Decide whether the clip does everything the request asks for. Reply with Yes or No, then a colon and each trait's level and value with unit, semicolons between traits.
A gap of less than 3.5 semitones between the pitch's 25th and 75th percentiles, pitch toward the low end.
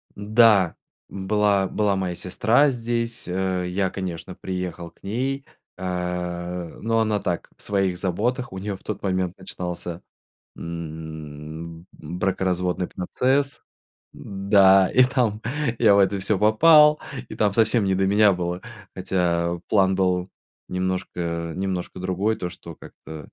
Yes: average, 3.0 semitones; very low, 95 Hz